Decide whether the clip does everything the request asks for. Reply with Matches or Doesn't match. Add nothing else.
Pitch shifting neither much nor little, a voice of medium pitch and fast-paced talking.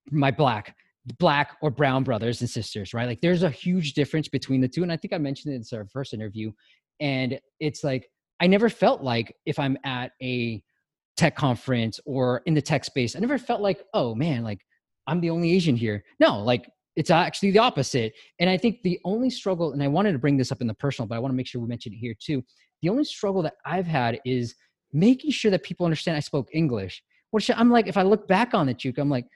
Doesn't match